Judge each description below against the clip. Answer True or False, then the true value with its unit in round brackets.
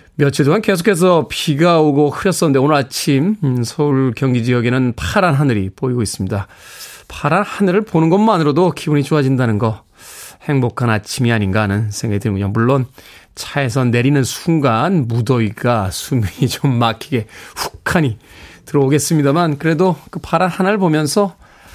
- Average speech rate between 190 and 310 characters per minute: False (335 characters per minute)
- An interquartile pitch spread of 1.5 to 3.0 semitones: False (5.3 semitones)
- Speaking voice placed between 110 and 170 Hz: True (140 Hz)